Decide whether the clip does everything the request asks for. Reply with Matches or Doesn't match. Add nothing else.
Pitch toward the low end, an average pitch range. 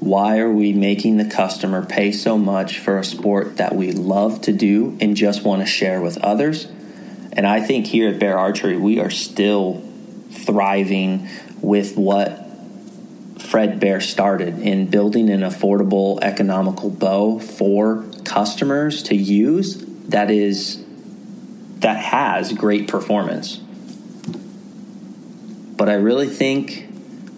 Doesn't match